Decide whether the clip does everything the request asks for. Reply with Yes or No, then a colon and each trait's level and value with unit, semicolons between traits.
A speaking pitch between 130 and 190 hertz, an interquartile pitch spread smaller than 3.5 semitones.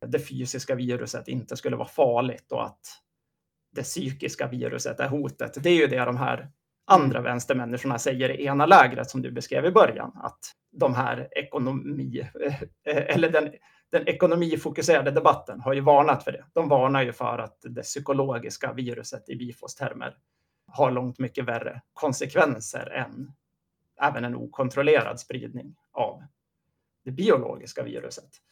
Yes: low, 135 Hz; narrow, 2.5 semitones